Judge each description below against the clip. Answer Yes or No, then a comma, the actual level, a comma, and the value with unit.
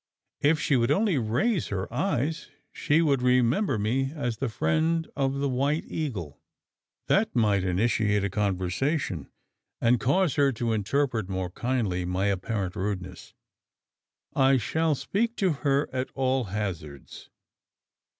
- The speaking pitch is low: Yes, low, 125 Hz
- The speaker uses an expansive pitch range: Yes, wide, 6.3 semitones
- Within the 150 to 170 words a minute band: No, slow, 135 wpm